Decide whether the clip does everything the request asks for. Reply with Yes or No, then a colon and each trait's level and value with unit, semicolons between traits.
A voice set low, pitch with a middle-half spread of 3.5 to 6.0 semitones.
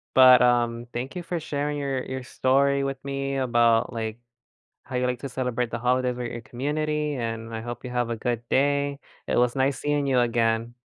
No: low, 125 Hz; narrow, 2.6 semitones